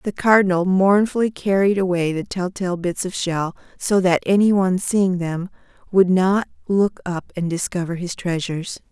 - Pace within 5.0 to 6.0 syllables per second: No, 4.7 syllables/s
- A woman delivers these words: Yes, female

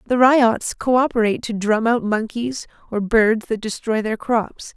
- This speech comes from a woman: Yes, female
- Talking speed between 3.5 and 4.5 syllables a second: Yes, 4.4 syllables/s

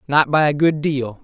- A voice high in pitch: No, medium, 145 Hz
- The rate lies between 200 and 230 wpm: No, fast, 245 wpm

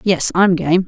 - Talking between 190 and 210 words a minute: Yes, fast, 205 wpm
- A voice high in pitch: No, medium, 180 Hz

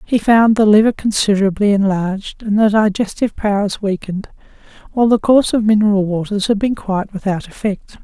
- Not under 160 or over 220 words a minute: Yes, average, 165 wpm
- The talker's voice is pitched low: No, high, 205 Hz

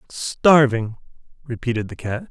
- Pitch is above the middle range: No, low, 125 Hz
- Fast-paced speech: No, slow, 105 wpm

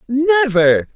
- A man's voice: Yes, male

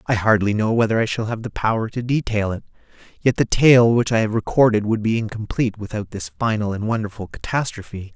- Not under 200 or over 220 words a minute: Yes, fast, 205 wpm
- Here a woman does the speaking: No, male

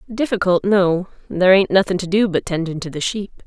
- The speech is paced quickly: Yes, fast, 210 wpm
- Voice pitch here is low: No, medium, 185 Hz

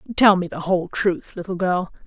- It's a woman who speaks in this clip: Yes, female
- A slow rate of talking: No, fast, 205 wpm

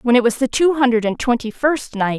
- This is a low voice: No, high, 245 Hz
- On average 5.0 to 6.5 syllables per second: Yes, 5.5 syllables/s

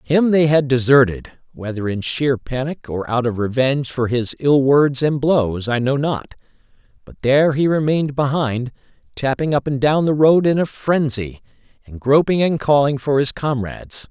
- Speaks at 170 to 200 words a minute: Yes, average, 180 wpm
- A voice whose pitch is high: No, low, 135 Hz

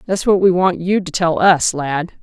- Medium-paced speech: No, fast, 245 wpm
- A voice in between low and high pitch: Yes, medium, 180 Hz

